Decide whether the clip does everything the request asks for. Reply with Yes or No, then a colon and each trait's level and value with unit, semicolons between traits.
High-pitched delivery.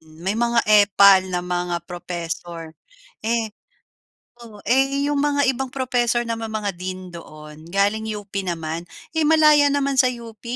Yes: high, 210 Hz